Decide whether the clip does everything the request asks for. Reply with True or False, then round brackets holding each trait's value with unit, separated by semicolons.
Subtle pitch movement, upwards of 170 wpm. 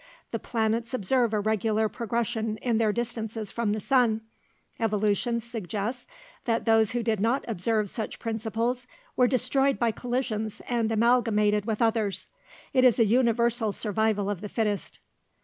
False (1.9 semitones; 150 wpm)